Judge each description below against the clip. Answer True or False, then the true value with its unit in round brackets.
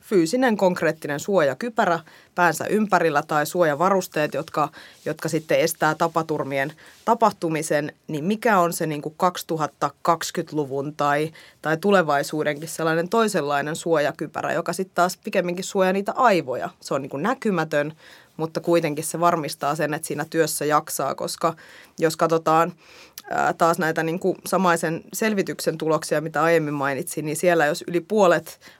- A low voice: False (165 Hz)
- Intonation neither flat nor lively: True (3.0 semitones)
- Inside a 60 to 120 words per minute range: False (135 wpm)